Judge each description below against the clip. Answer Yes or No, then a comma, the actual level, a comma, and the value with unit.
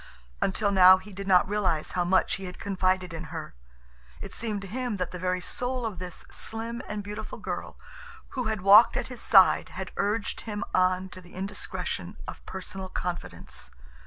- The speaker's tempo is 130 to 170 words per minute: No, average, 185 wpm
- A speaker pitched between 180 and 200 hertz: Yes, high, 190 Hz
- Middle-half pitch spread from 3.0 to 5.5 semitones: No, narrow, 2.4 semitones